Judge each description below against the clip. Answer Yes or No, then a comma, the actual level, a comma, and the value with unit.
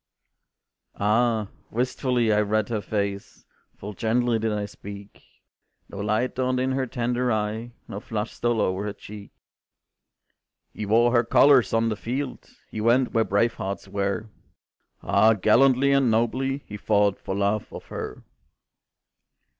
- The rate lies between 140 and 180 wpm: Yes, average, 145 wpm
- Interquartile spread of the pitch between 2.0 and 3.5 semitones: Yes, average, 2.9 semitones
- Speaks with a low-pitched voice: Yes, low, 110 Hz